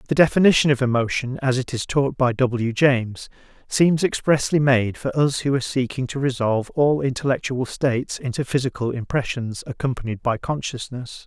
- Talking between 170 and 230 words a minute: No, average, 160 wpm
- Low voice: Yes, low, 130 Hz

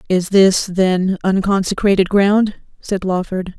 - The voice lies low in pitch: No, high, 190 Hz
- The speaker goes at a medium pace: No, slow, 115 wpm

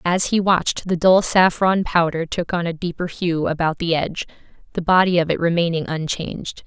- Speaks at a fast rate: No, average, 190 wpm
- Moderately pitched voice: Yes, medium, 170 Hz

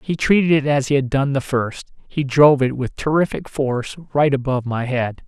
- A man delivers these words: Yes, male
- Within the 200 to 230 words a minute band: Yes, fast, 205 wpm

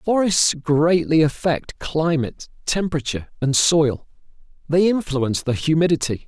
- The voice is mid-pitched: Yes, medium, 155 Hz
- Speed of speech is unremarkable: No, slow, 105 wpm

